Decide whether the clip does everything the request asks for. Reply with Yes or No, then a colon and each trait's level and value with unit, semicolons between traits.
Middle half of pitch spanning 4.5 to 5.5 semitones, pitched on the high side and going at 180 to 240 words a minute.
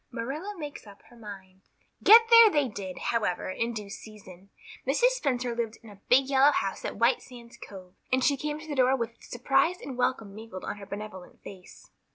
Yes: average, 5.1 semitones; high, 235 Hz; average, 200 wpm